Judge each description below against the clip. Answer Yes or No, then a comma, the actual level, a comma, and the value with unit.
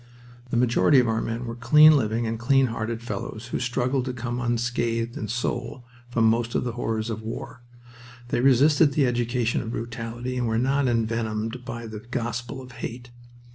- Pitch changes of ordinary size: No, narrow, 1.6 semitones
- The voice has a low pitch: Yes, low, 120 Hz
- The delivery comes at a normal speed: Yes, average, 180 wpm